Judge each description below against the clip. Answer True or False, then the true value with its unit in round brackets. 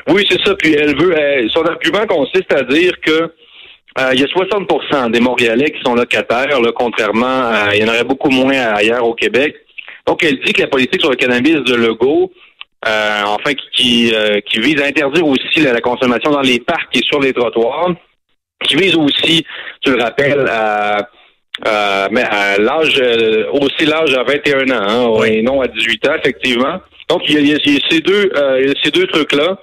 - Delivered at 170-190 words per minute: False (205 wpm)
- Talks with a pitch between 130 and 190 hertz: True (135 Hz)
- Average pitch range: False (5.7 semitones)